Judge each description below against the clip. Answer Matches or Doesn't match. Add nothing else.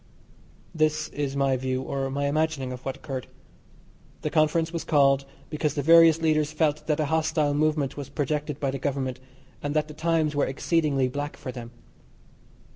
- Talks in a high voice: Doesn't match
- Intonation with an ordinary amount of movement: Doesn't match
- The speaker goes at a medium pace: Matches